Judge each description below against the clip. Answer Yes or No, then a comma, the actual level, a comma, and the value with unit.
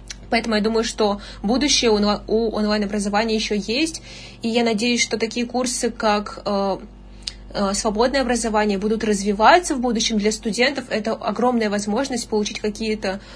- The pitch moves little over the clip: Yes, narrow, 2.3 semitones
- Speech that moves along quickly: No, average, 130 wpm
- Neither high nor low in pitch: No, high, 220 Hz